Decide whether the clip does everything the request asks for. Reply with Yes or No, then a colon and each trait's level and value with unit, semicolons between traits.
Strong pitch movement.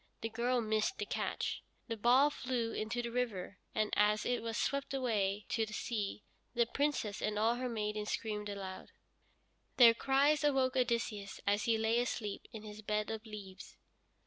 No: average, 2.7 semitones